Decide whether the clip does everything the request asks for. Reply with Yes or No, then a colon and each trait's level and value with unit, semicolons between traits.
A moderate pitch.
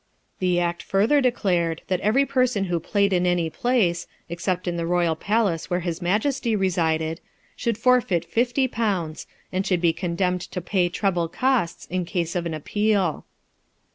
Yes: medium, 180 Hz